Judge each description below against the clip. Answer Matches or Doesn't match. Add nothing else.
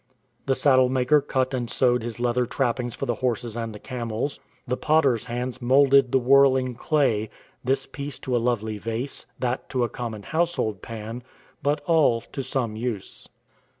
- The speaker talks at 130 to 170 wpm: Doesn't match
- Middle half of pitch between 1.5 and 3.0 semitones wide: Matches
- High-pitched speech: Doesn't match